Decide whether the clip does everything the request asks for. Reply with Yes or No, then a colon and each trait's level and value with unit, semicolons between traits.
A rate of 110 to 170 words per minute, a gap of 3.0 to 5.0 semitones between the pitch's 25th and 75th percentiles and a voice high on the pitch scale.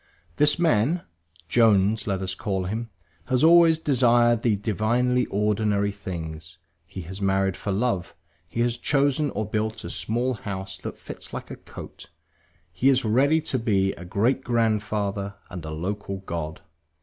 No: average, 155 wpm; average, 4.2 semitones; low, 105 Hz